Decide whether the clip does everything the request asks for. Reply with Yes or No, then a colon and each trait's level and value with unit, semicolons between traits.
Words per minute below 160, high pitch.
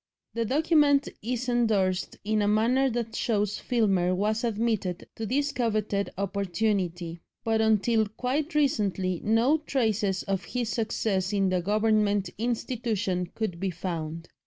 Yes: slow, 135 wpm; high, 215 Hz